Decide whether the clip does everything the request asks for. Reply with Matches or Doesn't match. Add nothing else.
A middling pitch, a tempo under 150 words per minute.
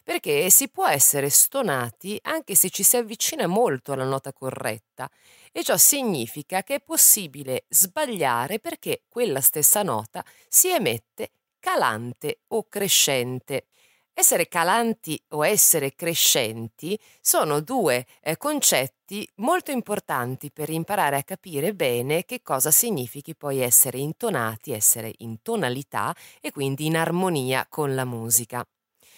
Matches